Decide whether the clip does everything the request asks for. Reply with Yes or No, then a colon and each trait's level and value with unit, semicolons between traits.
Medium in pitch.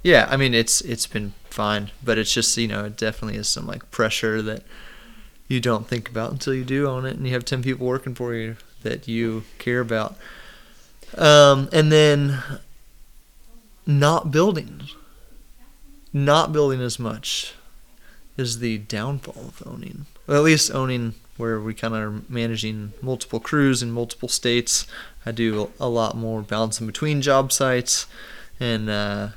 No: low, 120 Hz